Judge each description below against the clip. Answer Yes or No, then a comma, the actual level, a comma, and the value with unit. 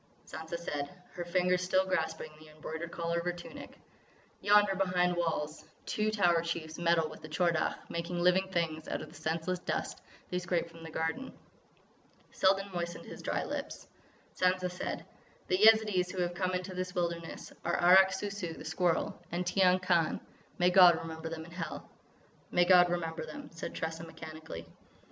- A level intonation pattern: Yes, narrow, 2.0 semitones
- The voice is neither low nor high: Yes, medium, 175 Hz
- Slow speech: No, average, 175 wpm